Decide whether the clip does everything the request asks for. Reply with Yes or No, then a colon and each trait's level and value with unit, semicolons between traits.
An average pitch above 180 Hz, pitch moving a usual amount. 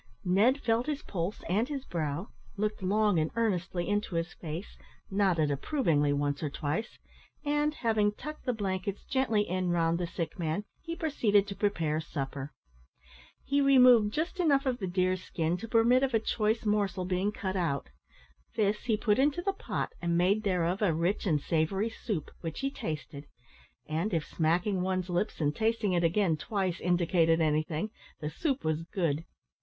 Yes: high, 190 Hz; average, 5.0 semitones